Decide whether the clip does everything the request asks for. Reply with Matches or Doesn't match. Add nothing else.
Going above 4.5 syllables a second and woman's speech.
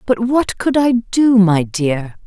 Doesn't match